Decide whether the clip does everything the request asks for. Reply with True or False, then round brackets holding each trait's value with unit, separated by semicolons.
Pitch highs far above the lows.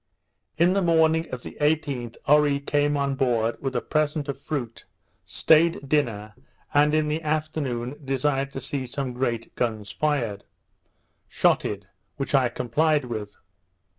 False (3.9 semitones)